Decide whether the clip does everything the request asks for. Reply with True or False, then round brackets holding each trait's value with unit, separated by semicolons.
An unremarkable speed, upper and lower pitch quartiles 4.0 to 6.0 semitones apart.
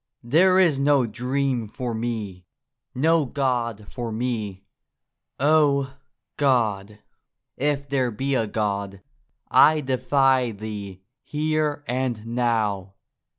False (105 wpm; 4.5 semitones)